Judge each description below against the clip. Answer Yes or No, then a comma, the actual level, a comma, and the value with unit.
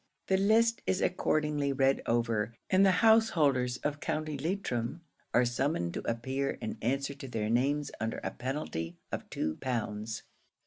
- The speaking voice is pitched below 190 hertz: Yes, low, 135 Hz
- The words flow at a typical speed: Yes, average, 150 wpm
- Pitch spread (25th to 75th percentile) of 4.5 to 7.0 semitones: Yes, average, 4.9 semitones